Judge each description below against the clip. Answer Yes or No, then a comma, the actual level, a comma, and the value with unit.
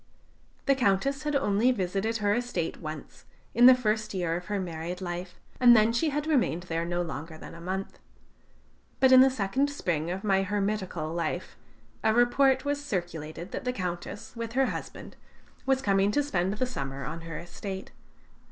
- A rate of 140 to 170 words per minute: No, average, 180 wpm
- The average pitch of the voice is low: No, high, 200 Hz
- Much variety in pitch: Yes, wide, 6.3 semitones